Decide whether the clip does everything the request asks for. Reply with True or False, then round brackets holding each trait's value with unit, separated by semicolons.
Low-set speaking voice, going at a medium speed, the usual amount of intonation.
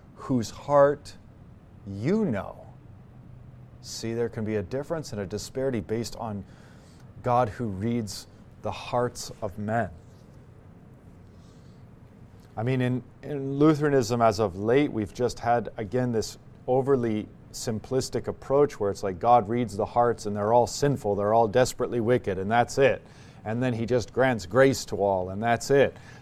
True (120 Hz; 155 wpm; 3.1 semitones)